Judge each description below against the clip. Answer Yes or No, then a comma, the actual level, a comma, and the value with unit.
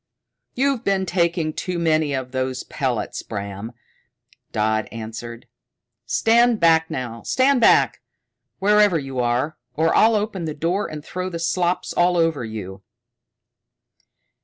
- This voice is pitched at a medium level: Yes, medium, 160 Hz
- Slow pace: Yes, slow, 125 wpm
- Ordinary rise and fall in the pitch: No, wide, 7.3 semitones